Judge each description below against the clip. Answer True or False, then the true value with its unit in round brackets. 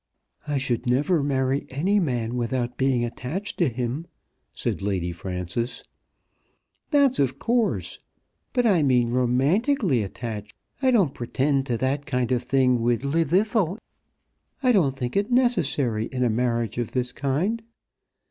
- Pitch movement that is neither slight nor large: False (6.1 semitones)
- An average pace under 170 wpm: True (140 wpm)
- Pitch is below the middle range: True (130 Hz)